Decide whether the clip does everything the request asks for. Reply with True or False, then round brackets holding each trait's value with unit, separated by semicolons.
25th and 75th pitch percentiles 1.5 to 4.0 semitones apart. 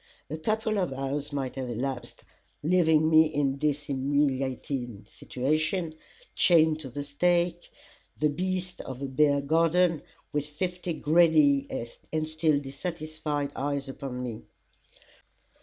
True (2.9 semitones)